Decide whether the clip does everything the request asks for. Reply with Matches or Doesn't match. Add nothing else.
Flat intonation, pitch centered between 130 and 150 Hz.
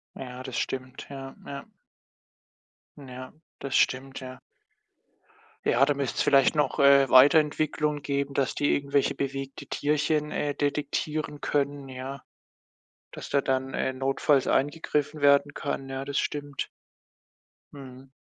Matches